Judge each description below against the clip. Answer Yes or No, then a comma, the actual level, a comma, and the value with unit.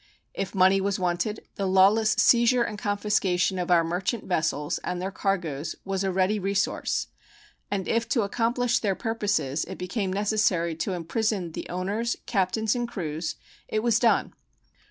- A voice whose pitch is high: Yes, high, 195 Hz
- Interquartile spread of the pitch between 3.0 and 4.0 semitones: Yes, average, 3.4 semitones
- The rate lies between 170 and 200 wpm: No, average, 155 wpm